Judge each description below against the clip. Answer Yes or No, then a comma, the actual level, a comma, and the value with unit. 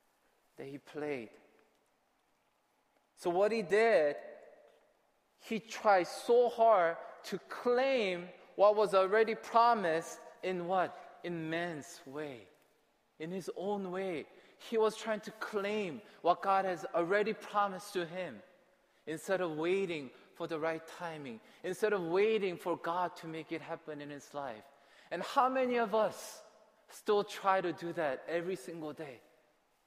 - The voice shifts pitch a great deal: No, average, 4.2 semitones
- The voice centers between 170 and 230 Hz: Yes, medium, 185 Hz